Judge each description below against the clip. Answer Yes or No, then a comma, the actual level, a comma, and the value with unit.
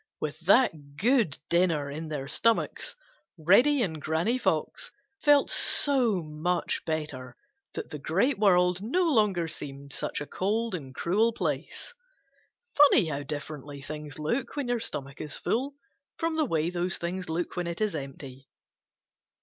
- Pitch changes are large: Yes, wide, 7.3 semitones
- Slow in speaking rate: No, average, 150 wpm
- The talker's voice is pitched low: No, medium, 175 Hz